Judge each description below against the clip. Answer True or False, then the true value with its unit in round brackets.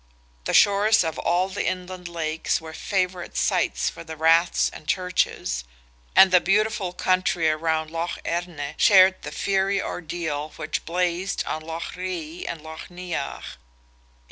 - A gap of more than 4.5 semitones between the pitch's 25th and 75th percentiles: False (2.5 semitones)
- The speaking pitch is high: False (175 Hz)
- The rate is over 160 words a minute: False (140 wpm)